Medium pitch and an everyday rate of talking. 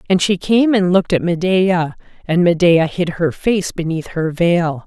Yes: medium, 175 Hz; average, 185 wpm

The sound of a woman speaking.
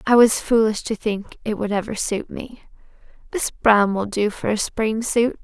Yes: female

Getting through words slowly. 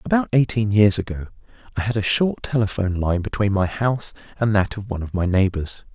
No: average, 200 wpm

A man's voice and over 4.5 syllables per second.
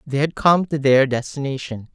Yes: male; 5.0 syllables/s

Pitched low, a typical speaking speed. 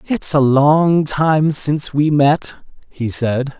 No: medium, 145 Hz; average, 150 wpm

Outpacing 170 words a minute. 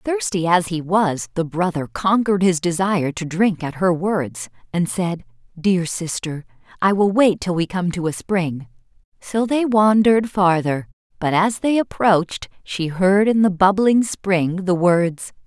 No: average, 165 wpm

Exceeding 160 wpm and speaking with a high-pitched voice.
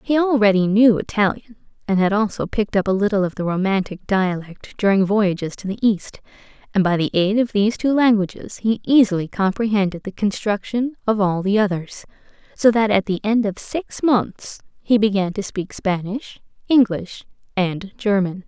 Yes: average, 170 wpm; high, 205 Hz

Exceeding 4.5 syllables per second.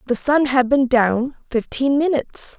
No: 4.4 syllables/s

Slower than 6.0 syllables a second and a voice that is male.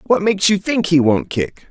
Yes: 5.0 syllables/s; male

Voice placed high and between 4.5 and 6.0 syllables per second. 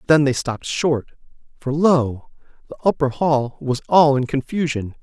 No: medium, 140 Hz; 4.6 syllables/s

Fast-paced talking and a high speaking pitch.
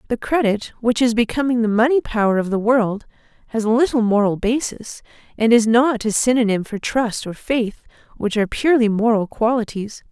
No: average, 170 wpm; high, 230 Hz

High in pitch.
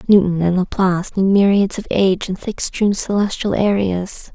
Yes: high, 195 Hz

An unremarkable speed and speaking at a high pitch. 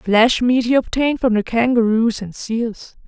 Yes: average, 175 wpm; high, 235 Hz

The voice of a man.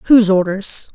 No: female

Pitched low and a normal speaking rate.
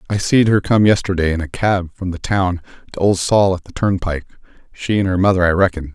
No: very low, 95 Hz; fast, 220 wpm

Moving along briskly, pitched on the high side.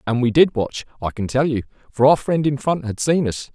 No: fast, 270 wpm; low, 130 Hz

